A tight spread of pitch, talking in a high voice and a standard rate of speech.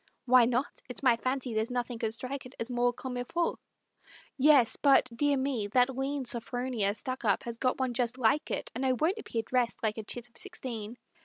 No: narrow, 2.3 semitones; very high, 250 Hz; fast, 210 wpm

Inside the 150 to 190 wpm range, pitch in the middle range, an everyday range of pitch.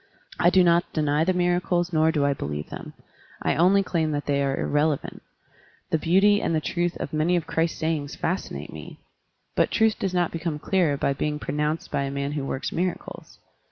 No: average, 200 wpm; medium, 160 Hz; average, 3.3 semitones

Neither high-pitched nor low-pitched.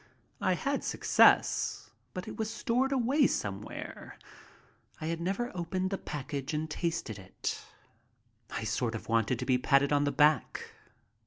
Yes: medium, 155 Hz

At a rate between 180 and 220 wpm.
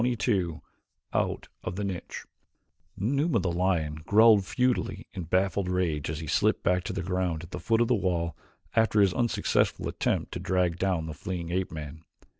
Yes: average, 185 wpm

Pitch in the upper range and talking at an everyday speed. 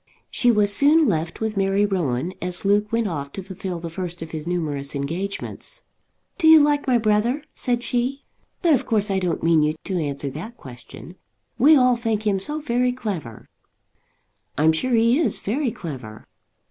Yes: high, 200 Hz; average, 180 wpm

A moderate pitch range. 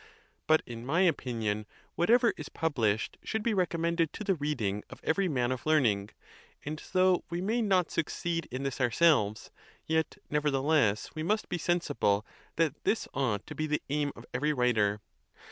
No: wide, 5.9 semitones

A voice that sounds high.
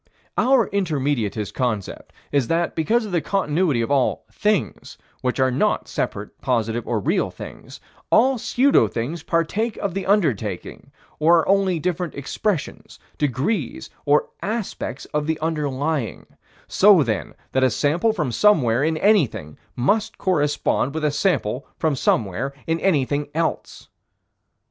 No: medium, 150 Hz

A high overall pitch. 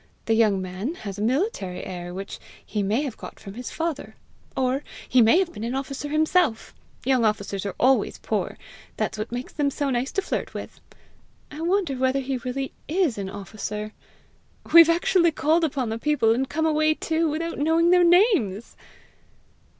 Yes: very high, 265 Hz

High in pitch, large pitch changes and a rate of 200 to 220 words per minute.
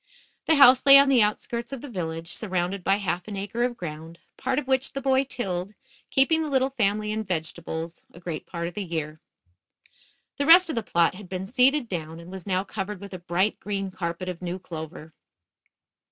Yes: high, 195 Hz; wide, 6.4 semitones; fast, 205 wpm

